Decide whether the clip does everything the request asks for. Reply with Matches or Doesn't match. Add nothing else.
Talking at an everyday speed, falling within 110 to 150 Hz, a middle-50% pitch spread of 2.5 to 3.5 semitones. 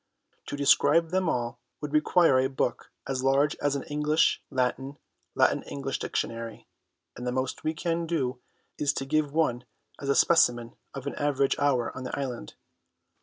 Matches